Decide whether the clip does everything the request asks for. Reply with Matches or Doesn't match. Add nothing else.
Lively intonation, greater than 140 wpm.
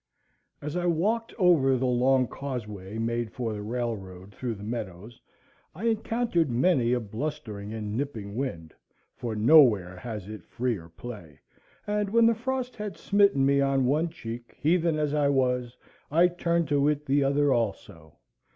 Matches